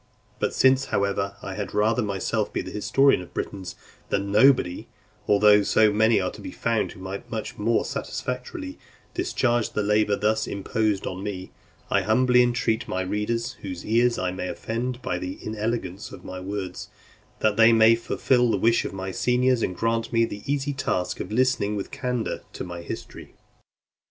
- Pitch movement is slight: No, average, 3.4 semitones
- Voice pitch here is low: Yes, low, 110 Hz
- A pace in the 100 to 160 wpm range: No, average, 180 wpm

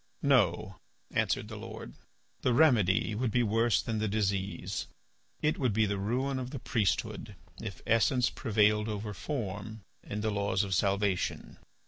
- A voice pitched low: Yes, low, 105 Hz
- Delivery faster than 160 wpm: No, average, 150 wpm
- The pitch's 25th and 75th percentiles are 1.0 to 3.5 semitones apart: Yes, average, 3.1 semitones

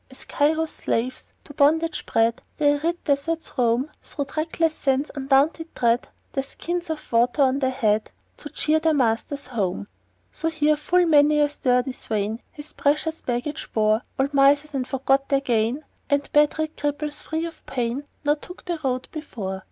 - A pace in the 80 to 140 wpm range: No, average, 170 wpm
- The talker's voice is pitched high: Yes, very high, 285 Hz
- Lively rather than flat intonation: No, average, 3.5 semitones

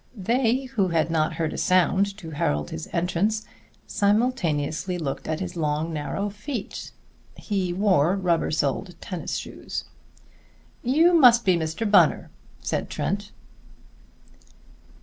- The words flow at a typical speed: No, slow, 125 wpm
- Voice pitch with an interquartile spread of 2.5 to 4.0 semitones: No, average, 4.7 semitones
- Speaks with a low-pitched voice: No, medium, 185 Hz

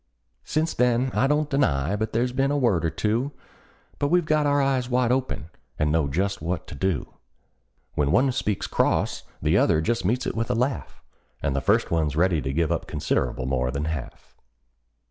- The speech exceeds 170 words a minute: Yes, average, 195 wpm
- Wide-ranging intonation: Yes, wide, 8.7 semitones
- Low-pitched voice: Yes, low, 110 Hz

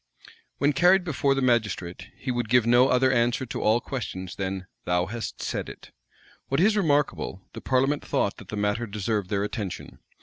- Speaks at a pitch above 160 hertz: No, low, 120 Hz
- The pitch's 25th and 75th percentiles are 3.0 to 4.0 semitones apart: No, average, 4.8 semitones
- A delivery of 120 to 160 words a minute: No, average, 180 wpm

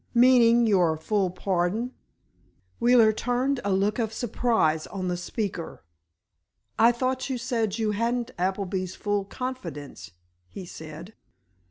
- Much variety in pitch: No, average, 4.6 semitones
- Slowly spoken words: Yes, slow, 125 wpm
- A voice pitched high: Yes, high, 215 Hz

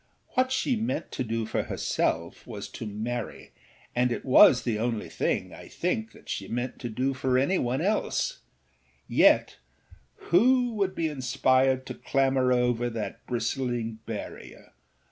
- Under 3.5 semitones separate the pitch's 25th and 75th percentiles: No, average, 4.6 semitones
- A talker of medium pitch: No, low, 125 Hz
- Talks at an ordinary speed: Yes, average, 150 wpm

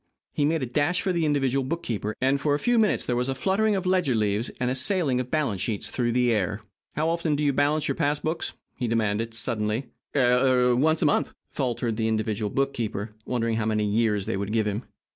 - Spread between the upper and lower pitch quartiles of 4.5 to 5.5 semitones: Yes, average, 4.8 semitones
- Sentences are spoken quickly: Yes, fast, 220 wpm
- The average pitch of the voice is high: No, low, 125 Hz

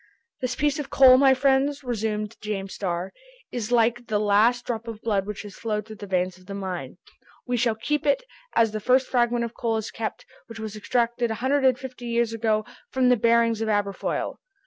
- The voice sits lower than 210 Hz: No, high, 230 Hz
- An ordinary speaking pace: No, fast, 210 wpm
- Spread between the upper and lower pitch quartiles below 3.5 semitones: Yes, average, 2.9 semitones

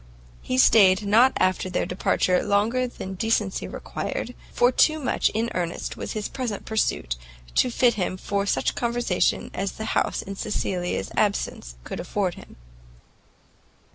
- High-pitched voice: Yes, high, 205 Hz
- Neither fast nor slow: Yes, average, 145 wpm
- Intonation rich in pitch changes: No, average, 4.0 semitones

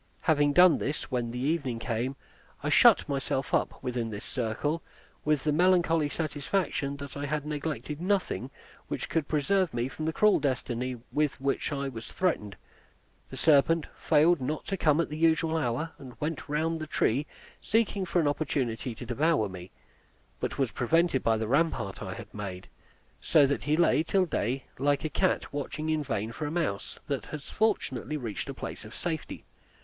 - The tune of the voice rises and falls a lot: No, average, 4.2 semitones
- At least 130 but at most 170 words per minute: No, average, 180 wpm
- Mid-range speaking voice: Yes, medium, 145 Hz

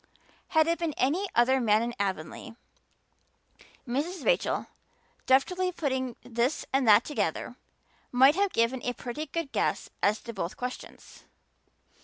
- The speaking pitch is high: Yes, very high, 260 Hz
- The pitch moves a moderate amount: Yes, average, 5.0 semitones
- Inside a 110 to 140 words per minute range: Yes, slow, 135 wpm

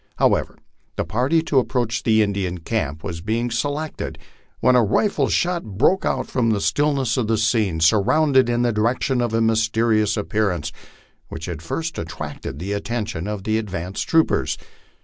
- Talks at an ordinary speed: Yes, average, 165 wpm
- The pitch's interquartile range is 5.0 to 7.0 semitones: No, average, 4.2 semitones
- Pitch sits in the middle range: No, low, 110 Hz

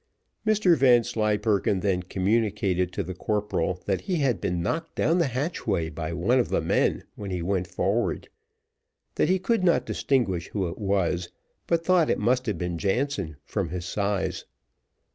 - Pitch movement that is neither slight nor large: No, wide, 6.1 semitones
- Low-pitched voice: Yes, low, 100 Hz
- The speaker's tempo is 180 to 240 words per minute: No, average, 170 wpm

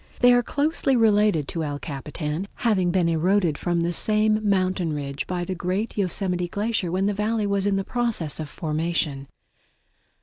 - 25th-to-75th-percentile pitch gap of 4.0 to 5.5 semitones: Yes, average, 4.3 semitones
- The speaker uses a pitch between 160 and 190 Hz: Yes, medium, 185 Hz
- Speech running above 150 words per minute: Yes, average, 165 wpm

